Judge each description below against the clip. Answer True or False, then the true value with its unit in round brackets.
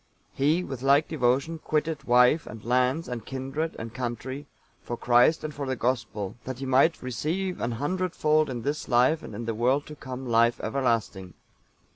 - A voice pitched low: True (130 Hz)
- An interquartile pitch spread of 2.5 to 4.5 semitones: True (4.0 semitones)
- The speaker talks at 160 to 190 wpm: True (180 wpm)